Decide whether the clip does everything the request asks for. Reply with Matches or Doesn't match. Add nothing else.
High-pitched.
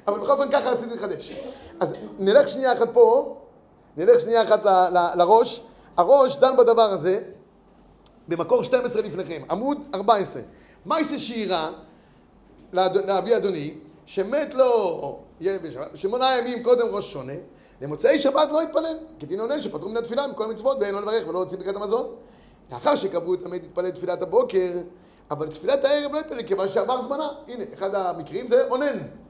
Matches